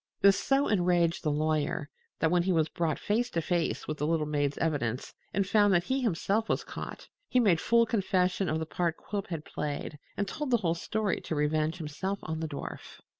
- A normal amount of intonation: Yes, average, 4.4 semitones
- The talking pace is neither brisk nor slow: No, fast, 210 wpm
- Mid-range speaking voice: Yes, medium, 170 Hz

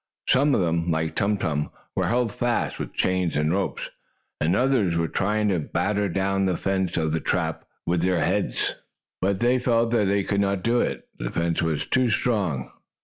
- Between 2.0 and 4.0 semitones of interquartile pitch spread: No, average, 4.4 semitones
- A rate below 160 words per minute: No, average, 200 wpm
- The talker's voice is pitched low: Yes, very low, 95 Hz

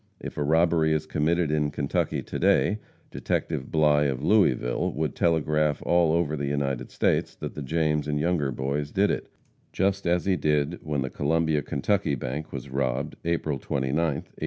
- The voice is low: Yes, very low, 75 Hz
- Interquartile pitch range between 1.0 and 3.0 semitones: Yes, average, 2.7 semitones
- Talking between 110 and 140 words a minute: No, average, 175 wpm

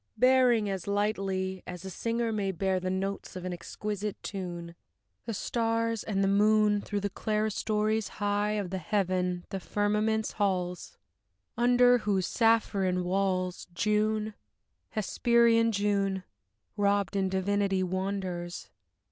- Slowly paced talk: Yes, slow, 125 wpm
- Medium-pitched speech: No, high, 200 Hz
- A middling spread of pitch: No, narrow, 2.3 semitones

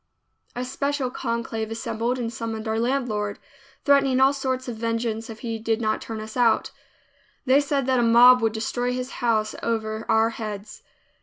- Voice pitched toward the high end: Yes, high, 230 Hz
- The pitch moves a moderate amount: No, narrow, 2.3 semitones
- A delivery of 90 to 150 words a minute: No, average, 170 wpm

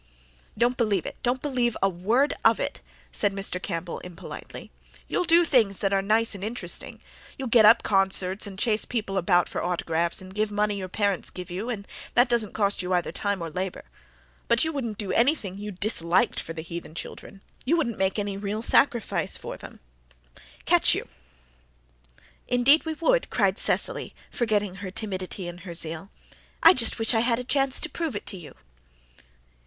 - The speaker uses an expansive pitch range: No, average, 4.2 semitones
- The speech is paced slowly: No, average, 185 wpm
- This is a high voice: Yes, high, 205 Hz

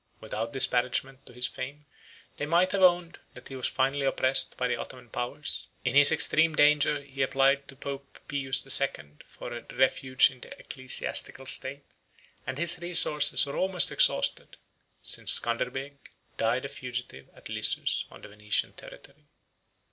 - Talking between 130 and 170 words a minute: Yes, average, 165 wpm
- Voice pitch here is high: No, low, 135 Hz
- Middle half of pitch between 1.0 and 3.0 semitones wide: Yes, narrow, 2.5 semitones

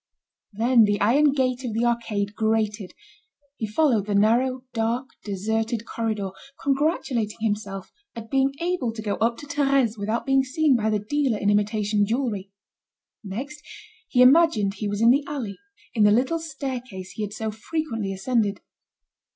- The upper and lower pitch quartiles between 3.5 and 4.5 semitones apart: Yes, average, 4.1 semitones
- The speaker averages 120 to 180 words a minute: Yes, average, 160 wpm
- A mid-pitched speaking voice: No, high, 225 Hz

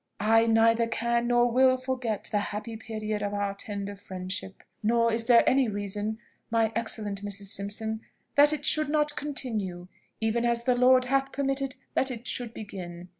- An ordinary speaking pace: Yes, average, 170 wpm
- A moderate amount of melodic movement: Yes, average, 3.6 semitones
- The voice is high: Yes, high, 225 Hz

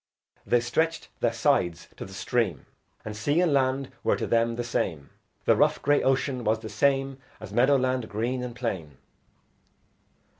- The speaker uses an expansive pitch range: No, average, 3.7 semitones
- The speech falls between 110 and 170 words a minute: Yes, average, 165 wpm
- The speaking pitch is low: Yes, low, 120 Hz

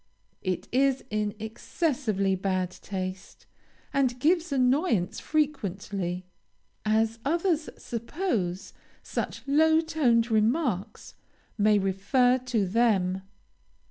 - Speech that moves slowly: Yes, slow, 90 wpm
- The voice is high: Yes, high, 230 Hz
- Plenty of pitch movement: Yes, wide, 6.2 semitones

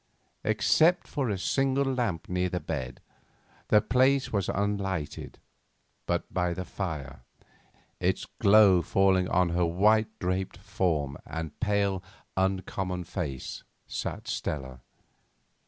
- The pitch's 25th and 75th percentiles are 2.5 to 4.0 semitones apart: Yes, average, 3.7 semitones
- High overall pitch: No, very low, 95 Hz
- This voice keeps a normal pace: No, slow, 115 wpm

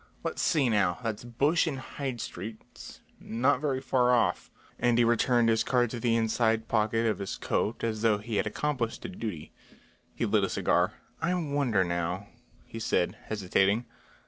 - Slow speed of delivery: No, average, 170 wpm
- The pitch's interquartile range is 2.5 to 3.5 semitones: Yes, average, 3.0 semitones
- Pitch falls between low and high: No, low, 115 Hz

